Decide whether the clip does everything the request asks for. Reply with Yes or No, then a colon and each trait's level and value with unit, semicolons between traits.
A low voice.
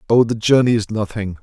Yes: low, 110 Hz